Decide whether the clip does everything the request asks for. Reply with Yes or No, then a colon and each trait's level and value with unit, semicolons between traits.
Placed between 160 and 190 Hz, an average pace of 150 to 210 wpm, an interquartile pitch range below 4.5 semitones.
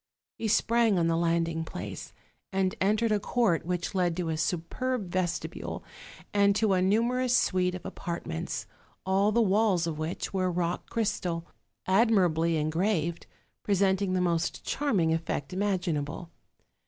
No: medium, 185 Hz; average, 140 wpm; average, 3.6 semitones